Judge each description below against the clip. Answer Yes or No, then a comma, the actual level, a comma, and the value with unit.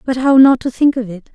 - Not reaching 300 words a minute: No, fast, 310 wpm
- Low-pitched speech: No, very high, 250 Hz